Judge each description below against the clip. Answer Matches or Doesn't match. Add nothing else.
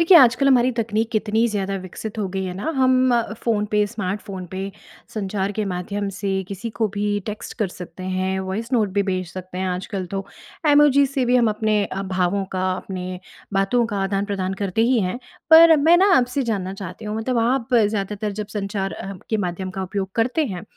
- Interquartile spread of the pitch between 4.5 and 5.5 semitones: Doesn't match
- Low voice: Doesn't match